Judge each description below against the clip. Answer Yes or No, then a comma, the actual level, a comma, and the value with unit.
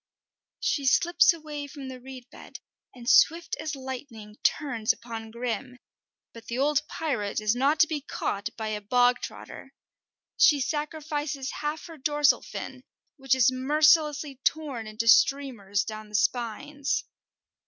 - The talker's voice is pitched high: Yes, very high, 265 Hz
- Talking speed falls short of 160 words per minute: Yes, average, 145 wpm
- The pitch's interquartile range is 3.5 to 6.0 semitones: Yes, average, 4.2 semitones